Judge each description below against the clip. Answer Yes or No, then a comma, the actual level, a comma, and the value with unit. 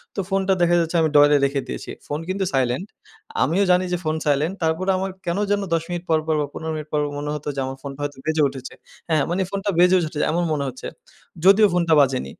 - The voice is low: No, medium, 160 Hz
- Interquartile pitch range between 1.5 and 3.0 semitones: No, average, 3.8 semitones